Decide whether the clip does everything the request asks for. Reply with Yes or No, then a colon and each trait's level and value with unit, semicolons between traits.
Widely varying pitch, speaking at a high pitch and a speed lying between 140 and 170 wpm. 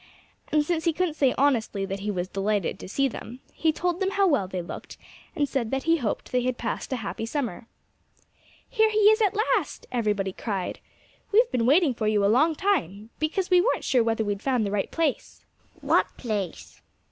No: wide, 8.0 semitones; very high, 250 Hz; fast, 205 wpm